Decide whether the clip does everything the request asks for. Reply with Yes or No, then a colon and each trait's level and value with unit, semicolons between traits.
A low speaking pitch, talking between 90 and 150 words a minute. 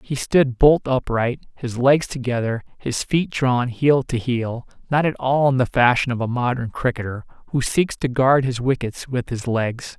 No: low, 125 Hz; average, 190 wpm